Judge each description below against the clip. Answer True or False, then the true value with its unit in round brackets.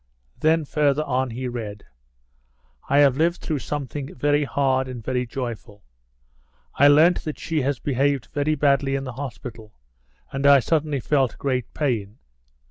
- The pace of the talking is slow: False (150 wpm)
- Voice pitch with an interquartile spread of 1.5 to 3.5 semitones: True (2.6 semitones)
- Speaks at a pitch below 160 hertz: True (135 Hz)